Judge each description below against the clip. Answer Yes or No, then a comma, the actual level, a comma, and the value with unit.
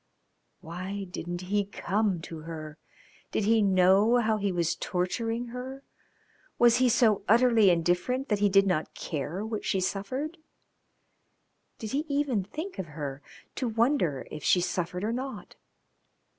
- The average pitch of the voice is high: Yes, high, 200 Hz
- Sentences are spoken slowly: No, average, 145 wpm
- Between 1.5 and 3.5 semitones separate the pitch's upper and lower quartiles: No, average, 4.9 semitones